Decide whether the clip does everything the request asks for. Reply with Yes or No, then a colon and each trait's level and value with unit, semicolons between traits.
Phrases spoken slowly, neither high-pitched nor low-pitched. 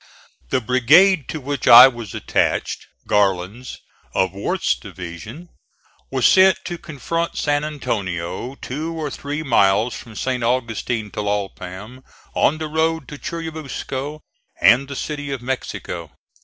No: slow, 130 wpm; low, 130 Hz